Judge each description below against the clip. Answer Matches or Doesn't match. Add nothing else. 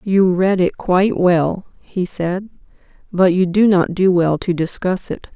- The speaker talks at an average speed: Matches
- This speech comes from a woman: Matches